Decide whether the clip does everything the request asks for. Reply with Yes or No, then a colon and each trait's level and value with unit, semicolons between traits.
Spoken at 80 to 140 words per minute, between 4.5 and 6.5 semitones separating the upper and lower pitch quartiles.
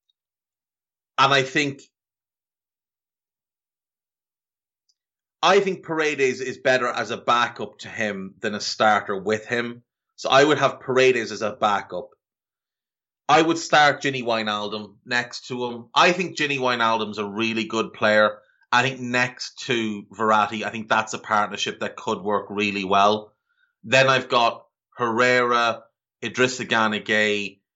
No: slow, 135 wpm; average, 3.6 semitones